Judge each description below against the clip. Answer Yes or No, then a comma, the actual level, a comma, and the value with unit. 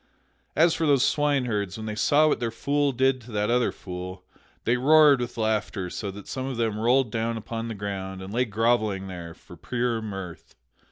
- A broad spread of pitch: No, average, 4.2 semitones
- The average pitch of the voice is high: No, low, 115 Hz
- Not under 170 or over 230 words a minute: Yes, average, 200 wpm